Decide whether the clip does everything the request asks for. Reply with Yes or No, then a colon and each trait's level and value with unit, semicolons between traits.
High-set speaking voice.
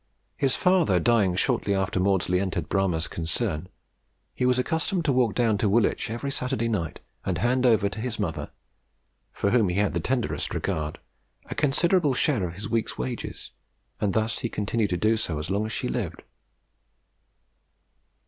No: low, 110 Hz